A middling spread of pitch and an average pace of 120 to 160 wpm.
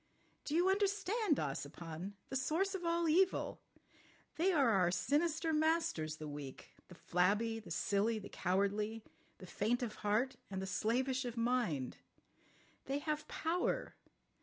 No: wide, 9.0 semitones; slow, 135 wpm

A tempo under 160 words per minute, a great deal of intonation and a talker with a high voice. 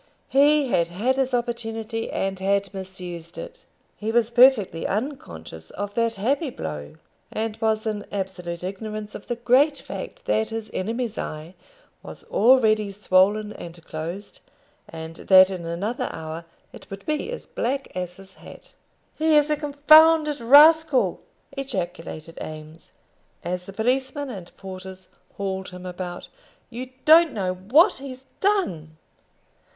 Yes: average, 140 wpm; wide, 6.1 semitones; high, 210 Hz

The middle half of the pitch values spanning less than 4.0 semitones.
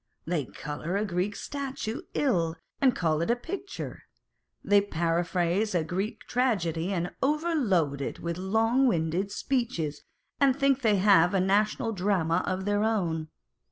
No: wide, 5.6 semitones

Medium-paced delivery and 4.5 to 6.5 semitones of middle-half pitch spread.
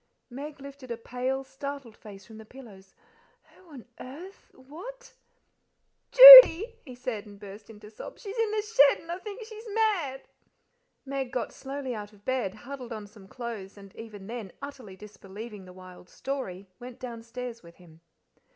Yes: average, 170 wpm; average, 5.1 semitones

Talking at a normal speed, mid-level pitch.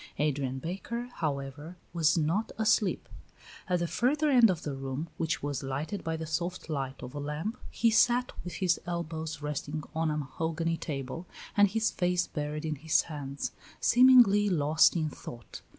Yes: average, 165 wpm; medium, 160 Hz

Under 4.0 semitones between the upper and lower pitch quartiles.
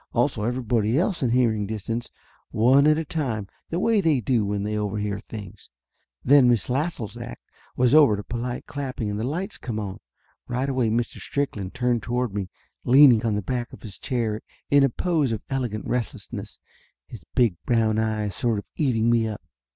Yes: average, 3.4 semitones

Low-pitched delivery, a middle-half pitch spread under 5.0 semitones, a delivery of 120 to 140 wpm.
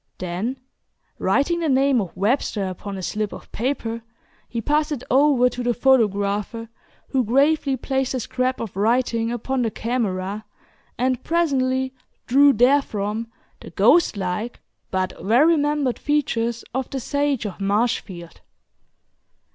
No: high, 245 Hz; average, 4.3 semitones; slow, 135 wpm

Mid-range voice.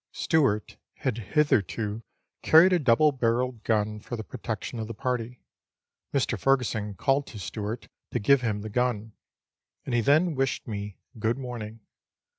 No: low, 115 Hz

